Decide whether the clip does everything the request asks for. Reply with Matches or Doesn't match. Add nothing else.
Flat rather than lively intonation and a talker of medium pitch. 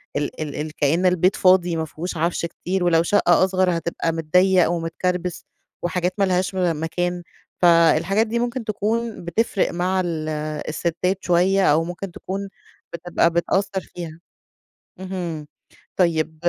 Matches